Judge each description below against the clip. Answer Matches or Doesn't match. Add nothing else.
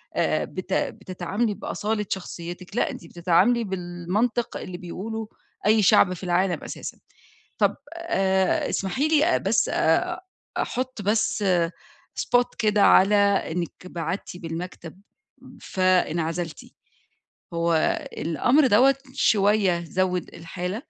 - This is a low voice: Doesn't match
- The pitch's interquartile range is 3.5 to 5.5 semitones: Matches